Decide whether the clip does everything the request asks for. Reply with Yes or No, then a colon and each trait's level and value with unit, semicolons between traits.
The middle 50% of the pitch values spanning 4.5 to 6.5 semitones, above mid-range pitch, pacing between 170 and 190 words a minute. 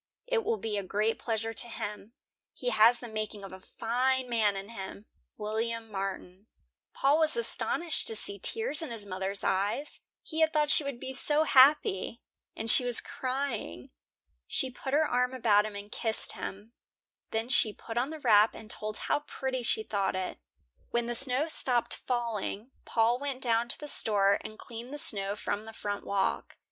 No: average, 4.0 semitones; high, 230 Hz; average, 185 wpm